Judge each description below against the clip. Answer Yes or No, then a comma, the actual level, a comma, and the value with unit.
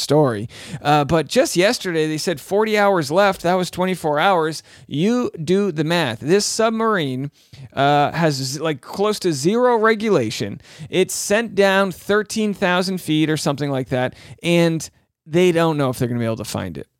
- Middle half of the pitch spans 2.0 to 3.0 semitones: No, wide, 5.4 semitones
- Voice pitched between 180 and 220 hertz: No, medium, 165 Hz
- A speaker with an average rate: Yes, average, 175 wpm